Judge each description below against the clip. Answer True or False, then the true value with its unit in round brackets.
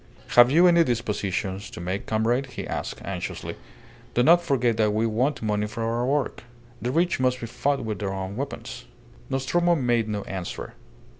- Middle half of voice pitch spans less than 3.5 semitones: False (4.5 semitones)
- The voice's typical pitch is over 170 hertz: False (120 Hz)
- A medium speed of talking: True (175 wpm)